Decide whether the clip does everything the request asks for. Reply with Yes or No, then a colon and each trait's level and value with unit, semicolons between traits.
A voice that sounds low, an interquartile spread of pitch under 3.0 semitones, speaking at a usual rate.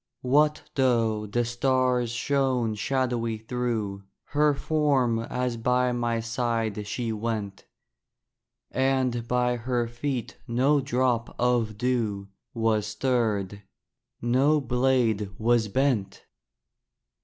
No: low, 120 Hz; narrow, 2.4 semitones; slow, 100 wpm